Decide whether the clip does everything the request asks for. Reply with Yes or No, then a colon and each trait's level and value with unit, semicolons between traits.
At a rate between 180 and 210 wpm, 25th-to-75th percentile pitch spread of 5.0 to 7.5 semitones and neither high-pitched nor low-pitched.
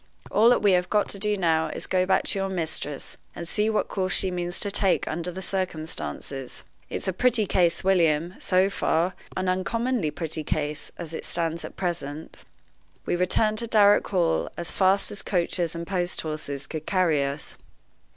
No: average, 190 wpm; average, 3.2 semitones; medium, 180 Hz